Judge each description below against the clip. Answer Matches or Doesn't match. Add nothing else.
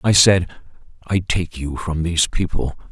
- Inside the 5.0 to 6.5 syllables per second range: Doesn't match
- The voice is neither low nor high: Doesn't match